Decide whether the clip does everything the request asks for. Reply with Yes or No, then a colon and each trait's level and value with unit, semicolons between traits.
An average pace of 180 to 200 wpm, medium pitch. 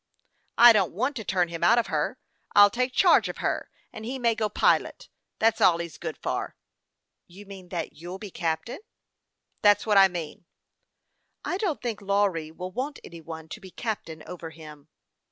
No: average, 195 wpm; high, 195 Hz